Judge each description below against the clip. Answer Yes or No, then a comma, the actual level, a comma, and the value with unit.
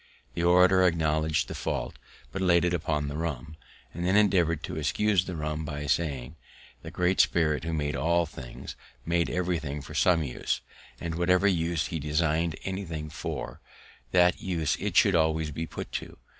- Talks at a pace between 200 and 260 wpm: No, average, 170 wpm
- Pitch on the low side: Yes, very low, 80 Hz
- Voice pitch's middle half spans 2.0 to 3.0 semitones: Yes, narrow, 2.4 semitones